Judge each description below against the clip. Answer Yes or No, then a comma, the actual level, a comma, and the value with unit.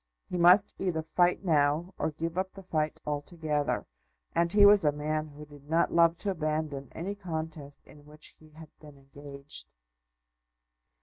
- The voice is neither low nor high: Yes, medium, 155 Hz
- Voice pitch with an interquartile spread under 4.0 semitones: Yes, average, 2.8 semitones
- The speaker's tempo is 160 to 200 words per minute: Yes, average, 165 wpm